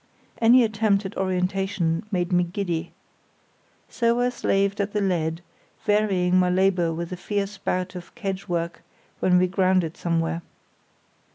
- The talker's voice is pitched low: No, medium, 185 Hz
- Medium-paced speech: Yes, average, 145 wpm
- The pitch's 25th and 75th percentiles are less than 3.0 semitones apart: Yes, narrow, 2.5 semitones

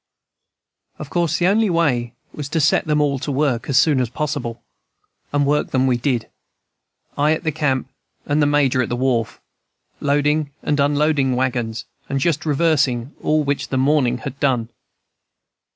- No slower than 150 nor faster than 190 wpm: Yes, average, 170 wpm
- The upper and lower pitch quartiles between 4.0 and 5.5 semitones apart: No, average, 2.8 semitones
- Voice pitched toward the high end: No, medium, 140 Hz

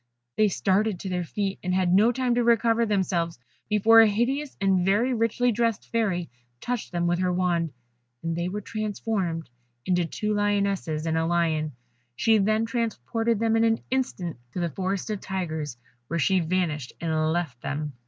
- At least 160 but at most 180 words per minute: Yes, average, 175 wpm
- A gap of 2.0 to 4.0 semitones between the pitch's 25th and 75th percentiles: No, average, 4.7 semitones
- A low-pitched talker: No, high, 190 Hz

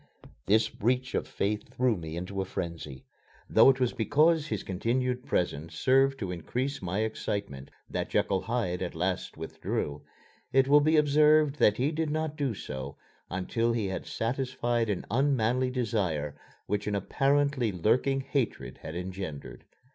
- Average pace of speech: Yes, average, 155 wpm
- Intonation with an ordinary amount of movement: No, wide, 6.5 semitones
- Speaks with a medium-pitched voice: No, low, 115 Hz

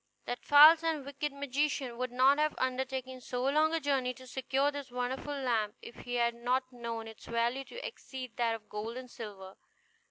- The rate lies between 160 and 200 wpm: Yes, average, 190 wpm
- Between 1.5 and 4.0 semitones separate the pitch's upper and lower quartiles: Yes, average, 2.9 semitones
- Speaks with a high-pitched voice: Yes, very high, 255 Hz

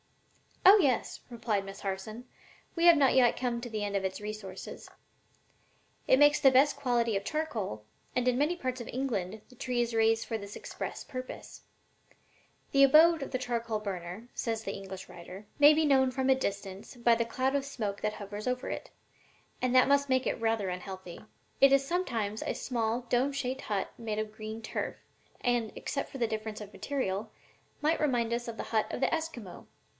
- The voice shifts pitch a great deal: No, average, 4.0 semitones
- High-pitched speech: Yes, high, 235 Hz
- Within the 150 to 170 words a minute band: No, average, 195 wpm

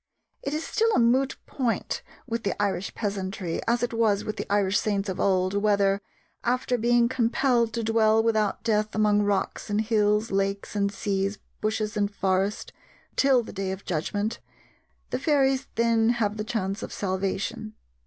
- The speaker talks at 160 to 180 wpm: Yes, average, 165 wpm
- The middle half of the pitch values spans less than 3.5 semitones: Yes, average, 2.7 semitones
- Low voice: No, high, 215 Hz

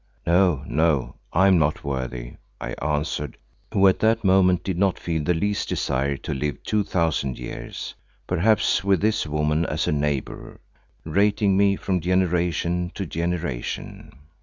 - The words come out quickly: No, average, 150 wpm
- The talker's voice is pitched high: No, very low, 85 Hz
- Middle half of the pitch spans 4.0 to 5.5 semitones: Yes, average, 4.4 semitones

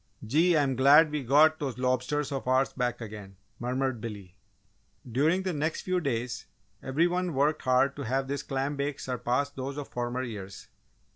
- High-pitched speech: No, low, 135 Hz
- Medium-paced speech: Yes, average, 170 wpm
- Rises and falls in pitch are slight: No, average, 3.0 semitones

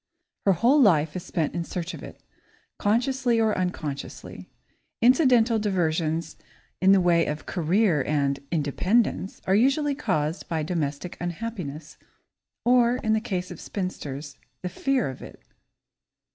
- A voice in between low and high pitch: Yes, medium, 180 Hz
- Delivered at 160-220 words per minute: No, slow, 135 wpm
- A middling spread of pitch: No, wide, 6.4 semitones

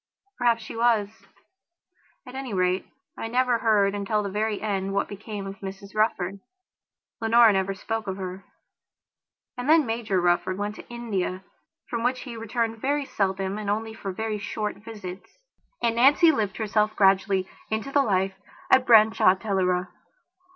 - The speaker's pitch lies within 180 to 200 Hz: No, high, 210 Hz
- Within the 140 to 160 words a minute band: Yes, average, 155 wpm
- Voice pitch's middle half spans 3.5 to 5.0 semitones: No, average, 2.9 semitones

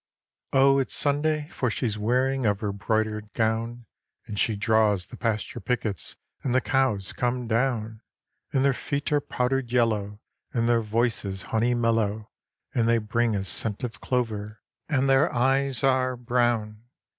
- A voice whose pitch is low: Yes, low, 115 Hz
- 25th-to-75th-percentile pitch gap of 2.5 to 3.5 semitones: Yes, average, 3.2 semitones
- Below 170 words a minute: Yes, average, 155 wpm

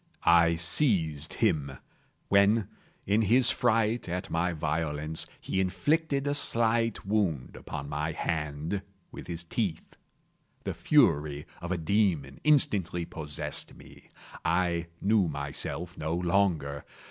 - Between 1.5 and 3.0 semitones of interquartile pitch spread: No, average, 5.3 semitones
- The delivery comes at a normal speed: No, slow, 120 wpm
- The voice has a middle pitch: No, very low, 85 Hz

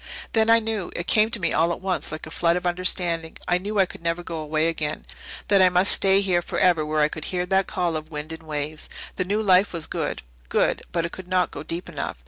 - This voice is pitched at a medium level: Yes, medium, 175 Hz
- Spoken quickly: Yes, fast, 255 wpm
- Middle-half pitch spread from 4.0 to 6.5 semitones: No, average, 2.8 semitones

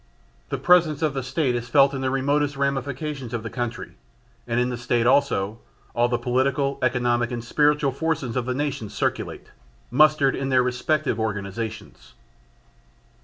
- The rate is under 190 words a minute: Yes, average, 160 wpm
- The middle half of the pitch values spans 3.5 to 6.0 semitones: No, average, 2.9 semitones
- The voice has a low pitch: Yes, low, 130 Hz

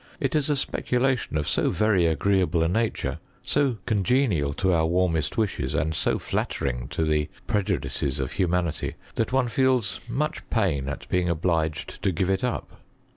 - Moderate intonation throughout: No, wide, 6.6 semitones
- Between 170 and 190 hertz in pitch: No, very low, 95 Hz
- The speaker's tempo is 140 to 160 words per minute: No, average, 170 wpm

